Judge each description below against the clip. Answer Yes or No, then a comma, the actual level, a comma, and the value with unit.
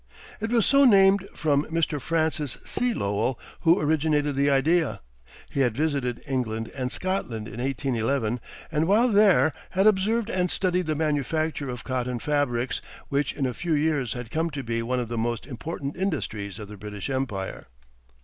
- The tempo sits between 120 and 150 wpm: No, average, 170 wpm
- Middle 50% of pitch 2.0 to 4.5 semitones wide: No, average, 5.2 semitones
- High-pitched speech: No, medium, 145 Hz